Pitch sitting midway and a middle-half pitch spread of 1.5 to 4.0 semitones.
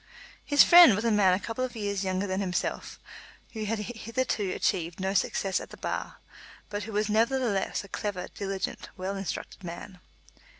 No: high, 200 Hz; average, 2.9 semitones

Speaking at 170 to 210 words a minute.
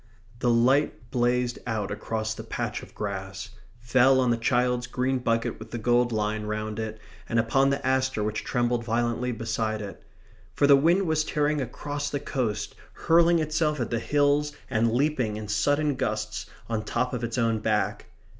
Yes: average, 175 wpm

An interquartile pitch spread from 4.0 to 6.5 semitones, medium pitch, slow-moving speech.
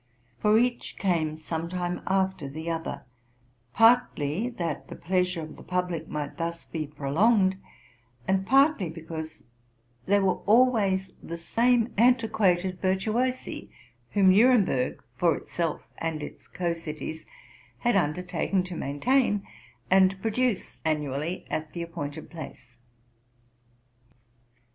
Yes: average, 4.5 semitones; medium, 180 Hz; slow, 115 wpm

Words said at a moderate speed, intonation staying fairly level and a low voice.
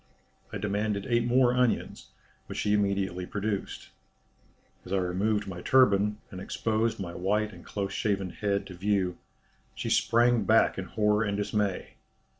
Yes: average, 150 wpm; narrow, 2.0 semitones; low, 105 Hz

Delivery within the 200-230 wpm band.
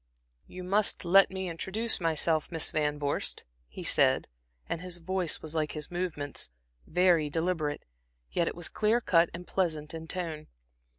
No: average, 160 wpm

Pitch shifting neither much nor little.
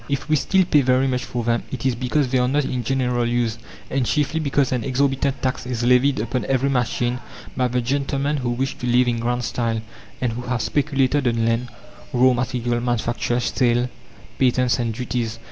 No: narrow, 1.9 semitones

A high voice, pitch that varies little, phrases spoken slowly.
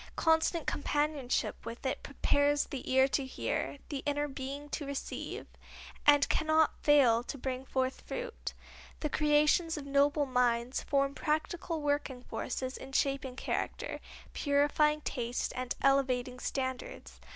Yes: very high, 280 Hz; narrow, 2.2 semitones; slow, 130 wpm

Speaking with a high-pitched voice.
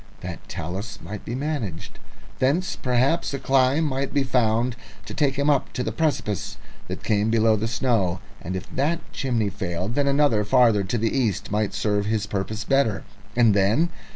No: low, 115 Hz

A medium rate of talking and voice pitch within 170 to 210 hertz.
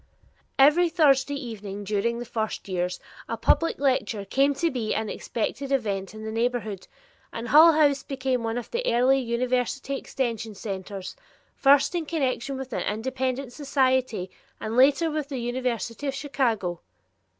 No: average, 150 wpm; very high, 255 Hz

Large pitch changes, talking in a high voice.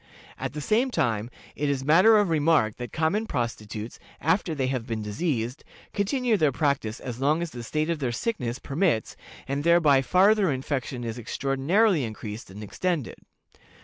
No: wide, 6.1 semitones; medium, 140 Hz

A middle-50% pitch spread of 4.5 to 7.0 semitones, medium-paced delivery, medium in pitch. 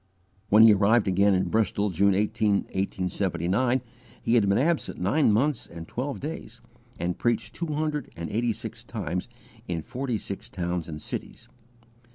No: average, 5.0 semitones; average, 165 wpm; low, 105 Hz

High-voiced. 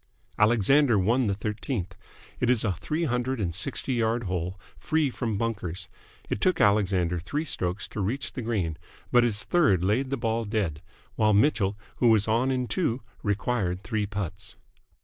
No: low, 110 Hz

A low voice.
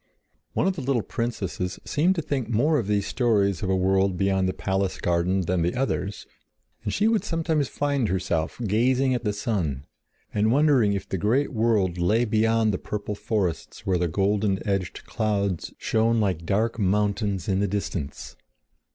Yes: low, 105 Hz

